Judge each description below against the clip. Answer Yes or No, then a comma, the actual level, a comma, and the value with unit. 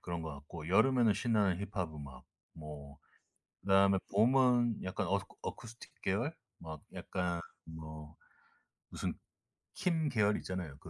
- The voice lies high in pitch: No, very low, 95 Hz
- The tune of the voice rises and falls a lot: Yes, wide, 6.1 semitones